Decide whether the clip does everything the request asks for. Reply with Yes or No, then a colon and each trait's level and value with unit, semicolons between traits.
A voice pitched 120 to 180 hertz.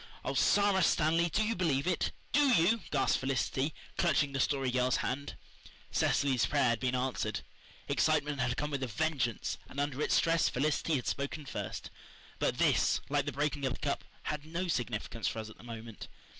Yes: medium, 140 Hz